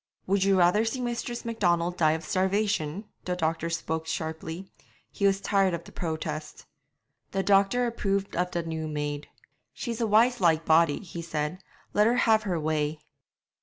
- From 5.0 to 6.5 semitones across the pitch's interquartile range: No, average, 4.2 semitones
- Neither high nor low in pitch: Yes, medium, 180 Hz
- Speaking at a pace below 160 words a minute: No, average, 165 wpm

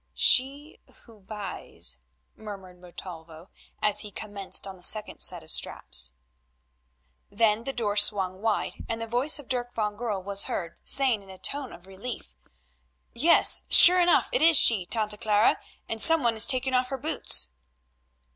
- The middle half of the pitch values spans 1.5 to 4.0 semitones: No, average, 4.6 semitones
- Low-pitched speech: No, high, 215 Hz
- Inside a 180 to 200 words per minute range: No, average, 165 wpm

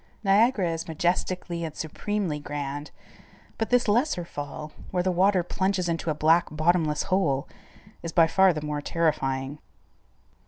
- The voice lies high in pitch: No, medium, 170 Hz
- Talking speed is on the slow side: No, average, 145 wpm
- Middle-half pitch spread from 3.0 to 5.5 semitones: Yes, average, 3.7 semitones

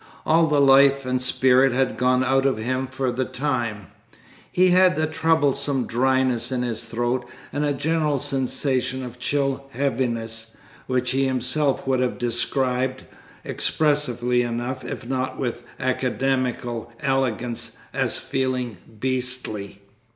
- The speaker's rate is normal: No, slow, 130 wpm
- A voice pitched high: No, low, 130 Hz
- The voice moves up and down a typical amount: No, narrow, 1.8 semitones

